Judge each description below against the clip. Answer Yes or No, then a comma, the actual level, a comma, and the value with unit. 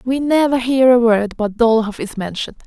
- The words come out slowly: No, fast, 205 wpm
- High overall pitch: Yes, high, 235 Hz